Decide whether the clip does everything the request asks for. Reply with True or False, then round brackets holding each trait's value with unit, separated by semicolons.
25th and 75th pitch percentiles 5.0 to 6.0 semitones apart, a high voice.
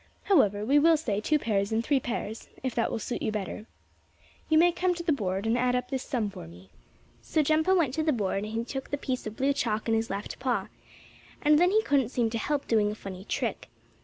True (5.6 semitones; 245 Hz)